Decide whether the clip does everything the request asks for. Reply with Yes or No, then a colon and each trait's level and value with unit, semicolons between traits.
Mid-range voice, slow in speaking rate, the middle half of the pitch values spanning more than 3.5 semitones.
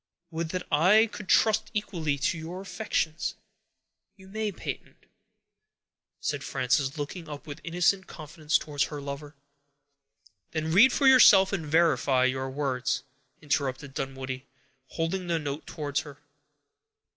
Yes: medium, 155 Hz; slow, 130 wpm; average, 4.5 semitones